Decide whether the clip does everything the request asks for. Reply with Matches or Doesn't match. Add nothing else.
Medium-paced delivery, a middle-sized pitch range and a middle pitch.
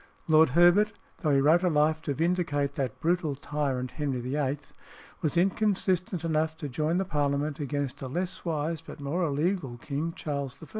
Matches